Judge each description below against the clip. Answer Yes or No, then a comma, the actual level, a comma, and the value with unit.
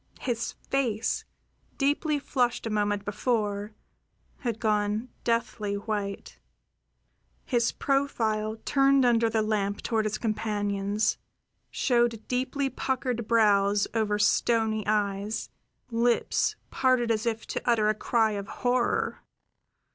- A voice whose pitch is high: Yes, high, 220 Hz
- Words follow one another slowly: Yes, slow, 110 wpm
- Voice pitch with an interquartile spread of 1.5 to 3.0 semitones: Yes, narrow, 2.6 semitones